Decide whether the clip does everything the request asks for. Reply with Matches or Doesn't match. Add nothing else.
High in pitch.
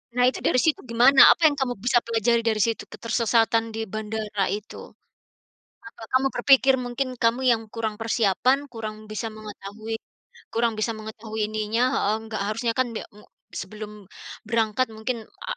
Matches